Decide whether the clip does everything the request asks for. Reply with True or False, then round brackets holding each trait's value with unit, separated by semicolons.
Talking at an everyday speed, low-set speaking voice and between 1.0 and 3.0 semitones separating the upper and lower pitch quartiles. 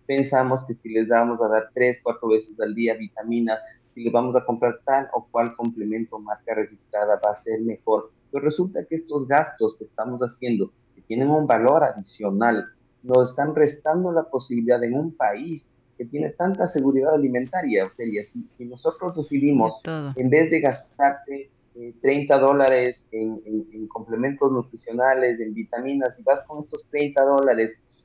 False (170 wpm; 125 Hz; 3.7 semitones)